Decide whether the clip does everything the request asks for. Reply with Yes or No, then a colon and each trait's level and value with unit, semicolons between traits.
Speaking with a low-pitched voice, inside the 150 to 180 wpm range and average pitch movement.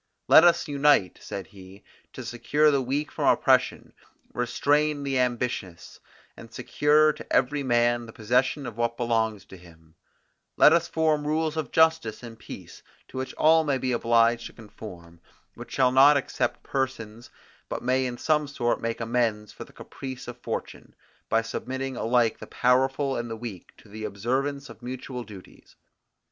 Yes: low, 125 Hz; average, 165 wpm; average, 3.8 semitones